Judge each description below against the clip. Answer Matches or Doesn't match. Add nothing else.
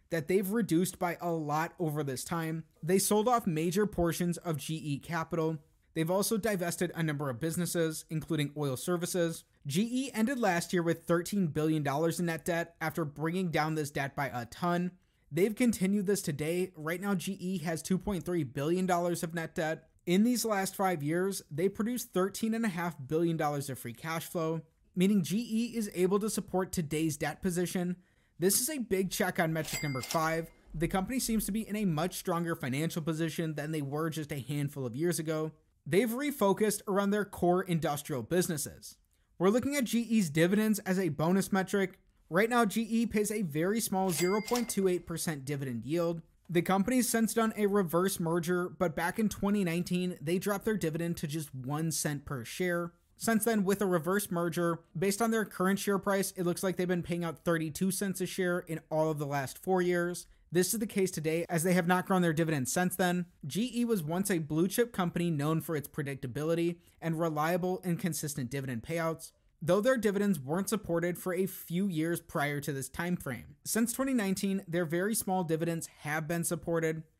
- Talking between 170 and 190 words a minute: Matches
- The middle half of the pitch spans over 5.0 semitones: Doesn't match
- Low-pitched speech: Doesn't match